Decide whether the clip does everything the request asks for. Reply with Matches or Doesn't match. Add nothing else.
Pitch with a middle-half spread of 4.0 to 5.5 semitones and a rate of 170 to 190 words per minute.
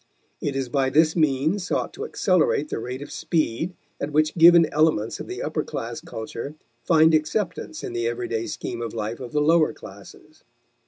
Matches